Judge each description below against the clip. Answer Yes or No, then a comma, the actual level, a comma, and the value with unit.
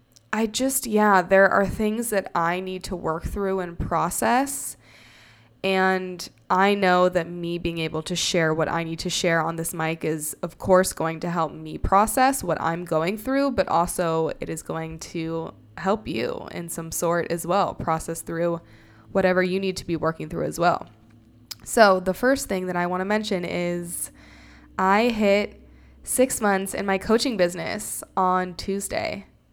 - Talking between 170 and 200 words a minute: Yes, average, 175 wpm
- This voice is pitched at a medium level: Yes, medium, 175 Hz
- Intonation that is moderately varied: Yes, average, 3.1 semitones